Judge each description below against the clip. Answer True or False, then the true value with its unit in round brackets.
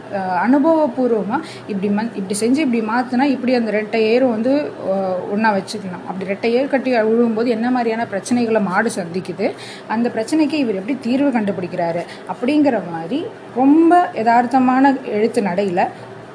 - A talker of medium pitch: False (230 Hz)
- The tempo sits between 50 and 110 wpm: False (130 wpm)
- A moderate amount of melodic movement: True (4.2 semitones)